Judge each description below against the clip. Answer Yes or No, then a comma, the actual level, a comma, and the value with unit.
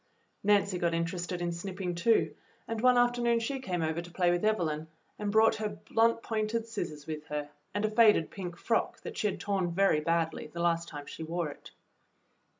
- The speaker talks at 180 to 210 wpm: Yes, average, 195 wpm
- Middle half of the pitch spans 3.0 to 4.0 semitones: No, average, 4.5 semitones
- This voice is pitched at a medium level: Yes, medium, 180 Hz